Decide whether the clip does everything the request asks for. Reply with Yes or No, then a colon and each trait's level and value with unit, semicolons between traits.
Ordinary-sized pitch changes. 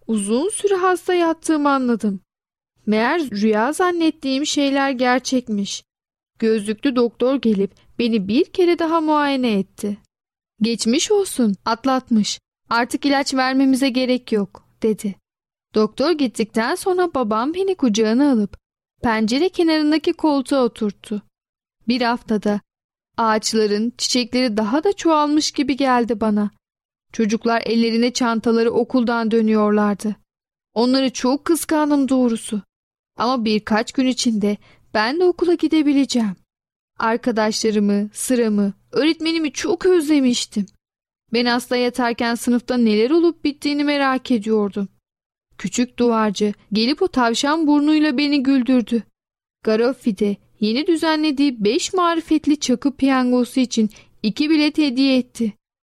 Yes: average, 4.9 semitones